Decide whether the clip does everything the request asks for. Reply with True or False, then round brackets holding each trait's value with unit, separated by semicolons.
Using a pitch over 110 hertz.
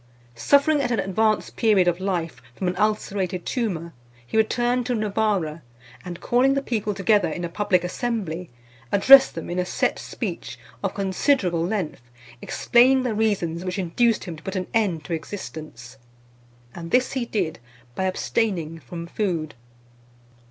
True (190 Hz)